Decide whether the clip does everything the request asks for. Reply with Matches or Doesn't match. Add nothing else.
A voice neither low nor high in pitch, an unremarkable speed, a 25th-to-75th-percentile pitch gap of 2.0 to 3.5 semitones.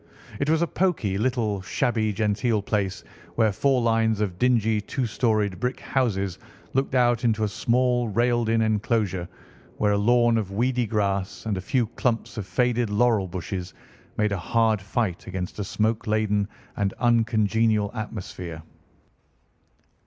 Doesn't match